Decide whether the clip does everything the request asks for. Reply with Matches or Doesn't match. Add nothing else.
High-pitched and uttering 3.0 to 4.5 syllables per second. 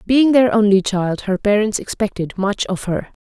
Doesn't match